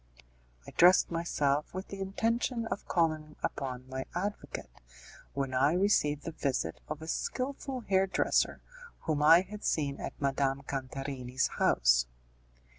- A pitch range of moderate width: No, wide, 5.8 semitones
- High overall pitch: No, medium, 155 Hz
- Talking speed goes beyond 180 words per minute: No, slow, 135 wpm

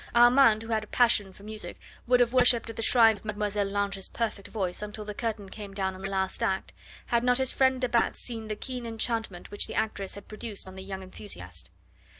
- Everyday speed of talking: No, fast, 225 wpm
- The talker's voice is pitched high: Yes, high, 215 Hz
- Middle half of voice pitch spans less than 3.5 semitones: Yes, average, 2.9 semitones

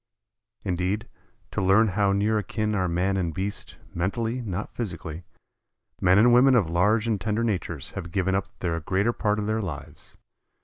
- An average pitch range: Yes, average, 3.2 semitones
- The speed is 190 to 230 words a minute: No, average, 170 wpm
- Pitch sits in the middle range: No, low, 100 Hz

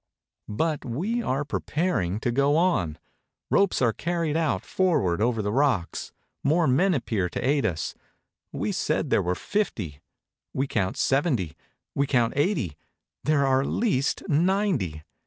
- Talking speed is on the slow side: No, average, 145 wpm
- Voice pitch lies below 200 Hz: Yes, low, 135 Hz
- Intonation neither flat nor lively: No, wide, 8.1 semitones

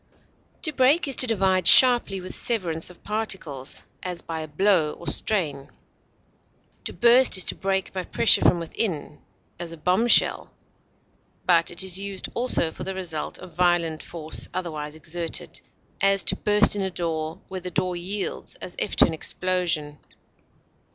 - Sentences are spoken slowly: No, average, 160 wpm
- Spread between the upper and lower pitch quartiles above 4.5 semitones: No, average, 3.3 semitones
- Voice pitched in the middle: Yes, medium, 180 Hz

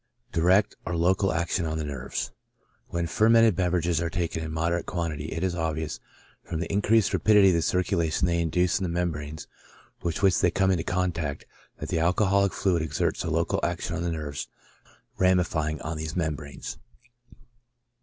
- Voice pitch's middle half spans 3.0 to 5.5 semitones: No, narrow, 2.5 semitones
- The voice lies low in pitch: Yes, very low, 85 Hz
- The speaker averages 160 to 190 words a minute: Yes, average, 175 wpm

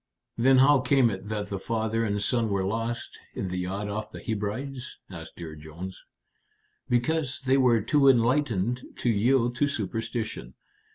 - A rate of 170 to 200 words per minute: No, average, 160 wpm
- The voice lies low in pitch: Yes, low, 115 Hz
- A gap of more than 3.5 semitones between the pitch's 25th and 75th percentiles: Yes, average, 4.1 semitones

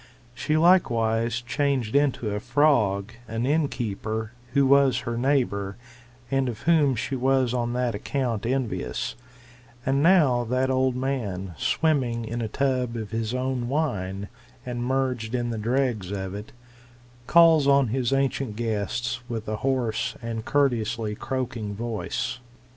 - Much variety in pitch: No, average, 3.3 semitones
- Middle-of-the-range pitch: No, low, 120 Hz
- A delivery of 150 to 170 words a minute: No, average, 140 wpm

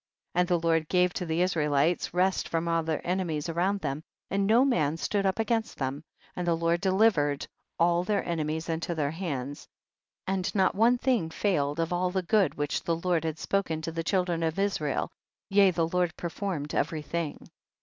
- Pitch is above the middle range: No, medium, 170 Hz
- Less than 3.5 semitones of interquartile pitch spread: Yes, average, 2.9 semitones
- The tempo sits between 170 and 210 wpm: Yes, average, 190 wpm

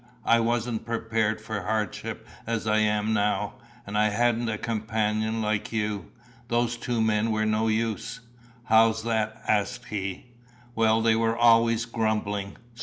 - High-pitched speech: No, low, 110 Hz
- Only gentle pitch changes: Yes, narrow, 1.2 semitones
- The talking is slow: No, average, 145 wpm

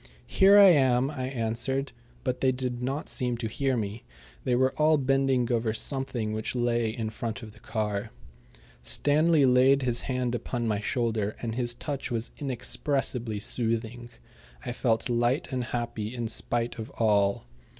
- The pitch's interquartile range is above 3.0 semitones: No, average, 2.7 semitones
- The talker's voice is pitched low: Yes, low, 120 Hz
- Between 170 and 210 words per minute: No, average, 160 wpm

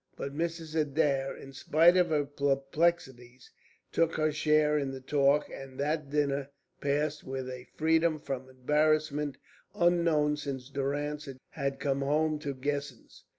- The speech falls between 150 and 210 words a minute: No, average, 140 wpm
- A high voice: No, medium, 145 Hz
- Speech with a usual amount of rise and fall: No, narrow, 2.0 semitones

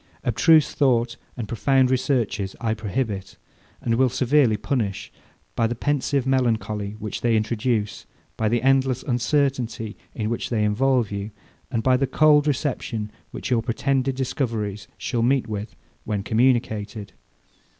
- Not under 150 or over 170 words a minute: No, average, 140 wpm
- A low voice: Yes, low, 120 Hz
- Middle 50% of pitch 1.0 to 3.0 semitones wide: No, average, 3.6 semitones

